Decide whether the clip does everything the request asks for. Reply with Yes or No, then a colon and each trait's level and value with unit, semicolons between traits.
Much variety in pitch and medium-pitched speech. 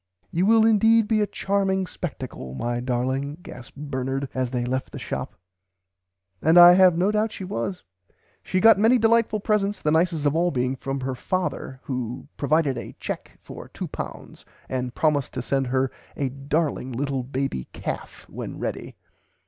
Yes: wide, 6.5 semitones; medium, 145 Hz